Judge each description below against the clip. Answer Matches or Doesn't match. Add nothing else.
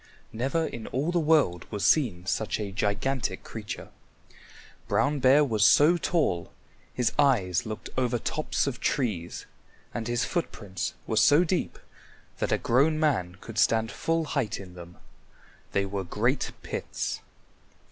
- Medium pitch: Doesn't match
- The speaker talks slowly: Doesn't match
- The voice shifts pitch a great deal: Matches